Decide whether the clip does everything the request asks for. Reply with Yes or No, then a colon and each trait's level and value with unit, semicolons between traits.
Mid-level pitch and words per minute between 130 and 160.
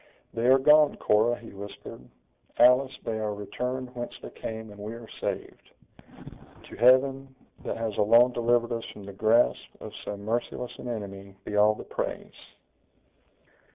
No: low, 115 Hz; average, 155 wpm